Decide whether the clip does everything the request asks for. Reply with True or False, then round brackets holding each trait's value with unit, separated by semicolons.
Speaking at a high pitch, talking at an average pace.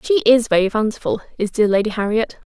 True (225 Hz; 190 wpm)